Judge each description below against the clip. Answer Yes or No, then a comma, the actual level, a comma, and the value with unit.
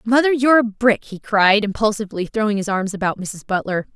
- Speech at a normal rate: Yes, average, 195 wpm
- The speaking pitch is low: No, high, 210 Hz